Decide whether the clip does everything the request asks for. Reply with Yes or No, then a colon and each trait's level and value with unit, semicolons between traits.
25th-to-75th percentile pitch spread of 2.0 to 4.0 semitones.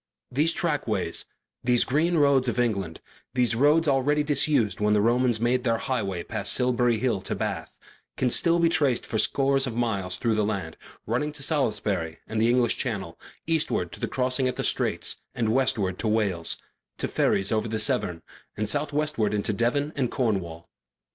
No: average, 4.4 semitones